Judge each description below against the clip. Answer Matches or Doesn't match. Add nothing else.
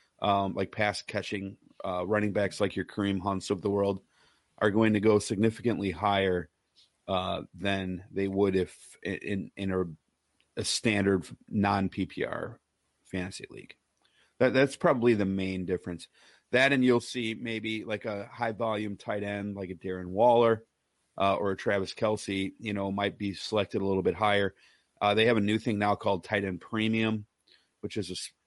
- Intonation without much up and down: Matches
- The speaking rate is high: Doesn't match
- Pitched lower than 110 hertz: Matches